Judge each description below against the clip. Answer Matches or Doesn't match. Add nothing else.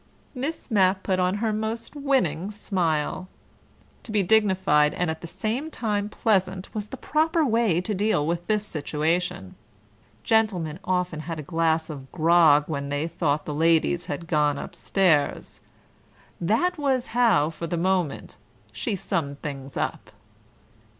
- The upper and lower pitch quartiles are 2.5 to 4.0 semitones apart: Doesn't match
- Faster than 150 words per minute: Doesn't match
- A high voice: Doesn't match